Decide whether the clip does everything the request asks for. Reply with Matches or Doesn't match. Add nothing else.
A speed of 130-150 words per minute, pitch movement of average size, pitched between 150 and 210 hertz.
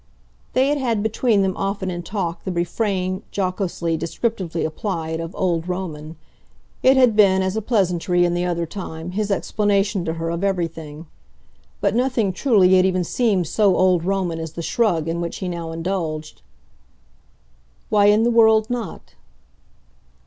Doesn't match